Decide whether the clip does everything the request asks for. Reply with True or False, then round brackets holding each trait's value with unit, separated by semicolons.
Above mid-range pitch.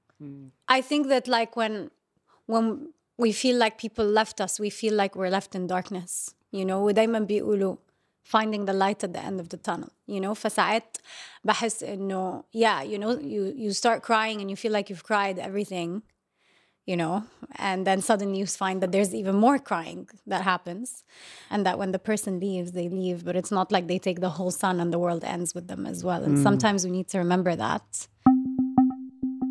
True (200 Hz)